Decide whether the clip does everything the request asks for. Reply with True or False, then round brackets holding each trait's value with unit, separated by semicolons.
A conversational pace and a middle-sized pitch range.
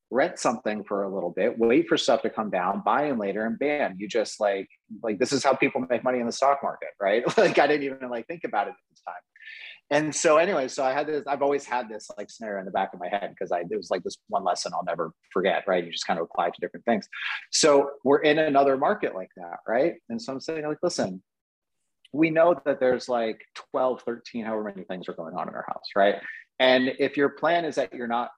False (255 wpm; 3.8 semitones)